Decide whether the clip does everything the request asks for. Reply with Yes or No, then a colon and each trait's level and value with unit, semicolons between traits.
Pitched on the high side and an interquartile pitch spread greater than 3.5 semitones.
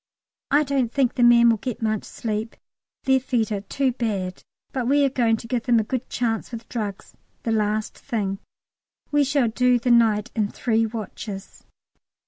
No: high, 230 Hz; narrow, 2.6 semitones